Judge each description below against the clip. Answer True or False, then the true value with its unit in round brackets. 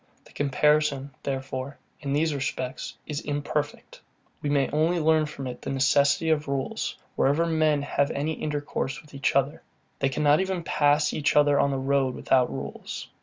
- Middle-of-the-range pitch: True (145 Hz)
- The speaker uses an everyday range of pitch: False (1.8 semitones)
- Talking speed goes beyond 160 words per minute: True (170 wpm)